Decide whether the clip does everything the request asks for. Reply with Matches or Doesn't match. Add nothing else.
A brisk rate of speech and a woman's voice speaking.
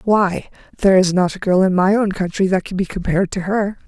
Matches